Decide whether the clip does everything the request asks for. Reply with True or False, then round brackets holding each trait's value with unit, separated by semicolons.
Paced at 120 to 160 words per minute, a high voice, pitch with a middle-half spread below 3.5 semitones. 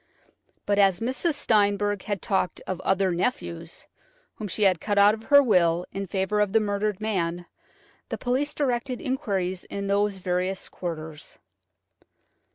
True (150 wpm; 200 Hz; 2.9 semitones)